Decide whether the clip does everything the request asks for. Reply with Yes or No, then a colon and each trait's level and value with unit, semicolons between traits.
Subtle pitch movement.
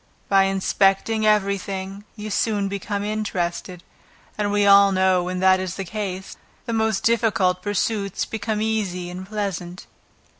Yes: narrow, 2.1 semitones